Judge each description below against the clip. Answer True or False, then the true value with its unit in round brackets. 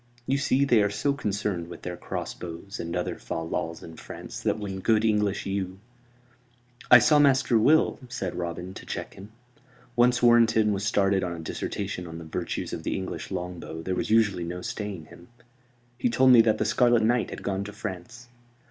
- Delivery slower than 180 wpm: False (195 wpm)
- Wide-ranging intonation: False (4.6 semitones)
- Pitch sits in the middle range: False (100 Hz)